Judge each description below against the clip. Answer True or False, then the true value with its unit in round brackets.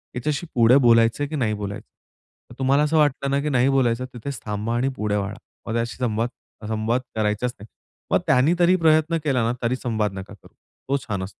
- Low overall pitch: True (120 Hz)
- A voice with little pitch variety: False (4.2 semitones)